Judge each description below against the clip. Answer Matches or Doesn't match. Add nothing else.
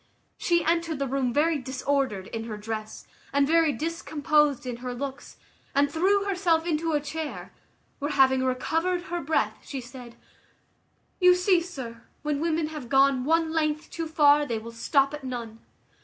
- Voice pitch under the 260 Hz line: Doesn't match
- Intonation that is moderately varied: Matches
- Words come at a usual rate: Matches